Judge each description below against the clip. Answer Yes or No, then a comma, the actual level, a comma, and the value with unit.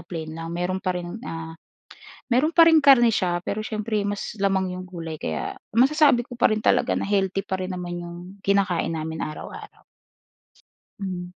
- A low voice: No, high, 190 Hz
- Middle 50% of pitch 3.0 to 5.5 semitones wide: Yes, average, 3.7 semitones